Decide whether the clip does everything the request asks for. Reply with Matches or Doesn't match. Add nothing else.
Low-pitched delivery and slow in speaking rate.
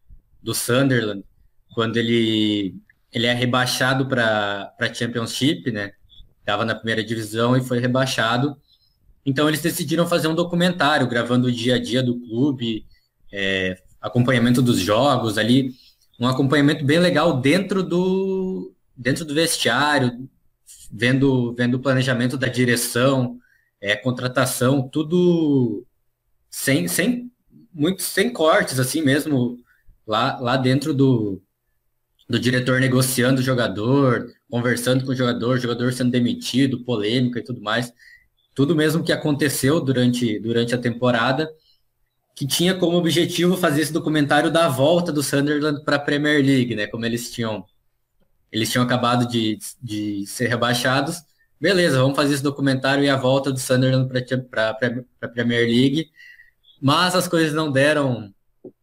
Doesn't match